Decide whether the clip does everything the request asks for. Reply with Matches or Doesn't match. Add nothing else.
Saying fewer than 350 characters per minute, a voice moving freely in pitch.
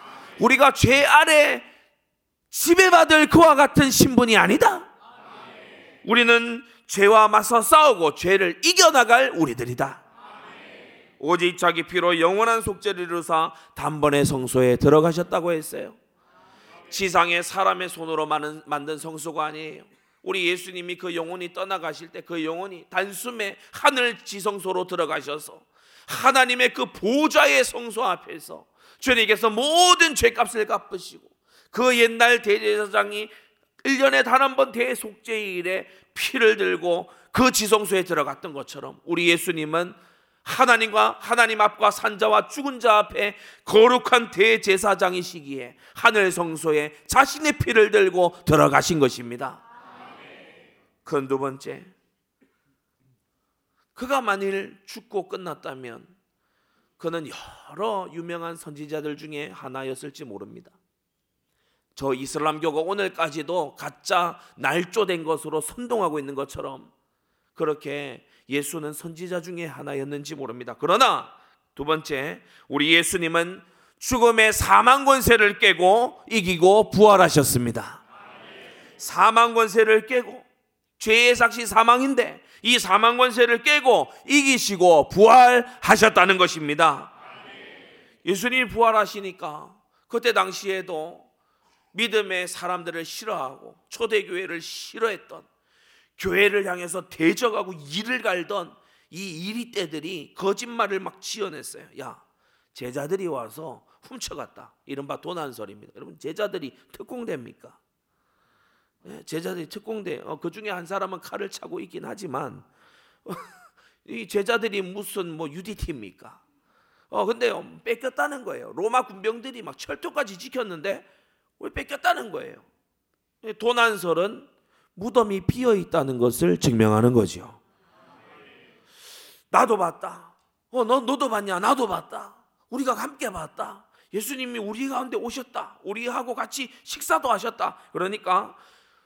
Matches